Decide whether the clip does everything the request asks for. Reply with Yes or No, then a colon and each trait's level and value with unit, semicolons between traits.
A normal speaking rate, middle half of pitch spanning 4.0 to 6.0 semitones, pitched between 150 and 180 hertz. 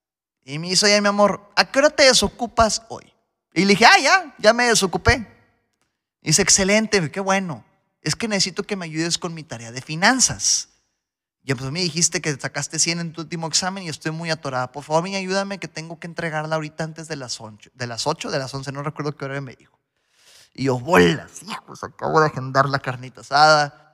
No: fast, 220 wpm; wide, 5.5 semitones; medium, 165 Hz